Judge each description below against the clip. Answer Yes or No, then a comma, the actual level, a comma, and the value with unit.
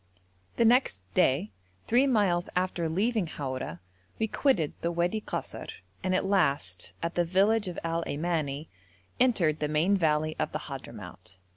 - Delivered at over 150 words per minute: No, average, 145 wpm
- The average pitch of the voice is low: No, medium, 175 Hz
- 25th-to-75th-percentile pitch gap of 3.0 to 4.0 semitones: No, average, 5.0 semitones